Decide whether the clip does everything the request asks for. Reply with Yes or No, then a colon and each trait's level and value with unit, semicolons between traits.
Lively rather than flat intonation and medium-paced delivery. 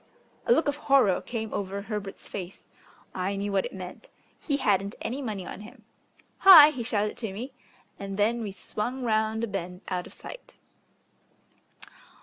No: average, 3.9 semitones; average, 165 wpm